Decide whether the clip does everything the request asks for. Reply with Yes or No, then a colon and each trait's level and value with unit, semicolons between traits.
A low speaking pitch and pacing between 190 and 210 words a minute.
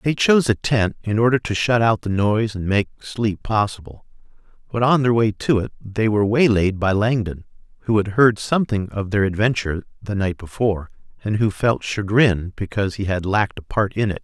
Yes: low, 105 Hz; average, 200 wpm